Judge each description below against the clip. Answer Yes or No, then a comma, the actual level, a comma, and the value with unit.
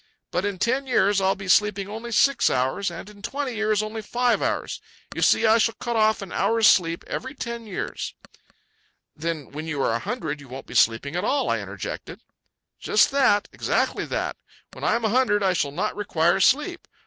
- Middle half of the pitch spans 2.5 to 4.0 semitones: No, average, 5.3 semitones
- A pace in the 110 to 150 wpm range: No, average, 200 wpm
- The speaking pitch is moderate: No, high, 210 Hz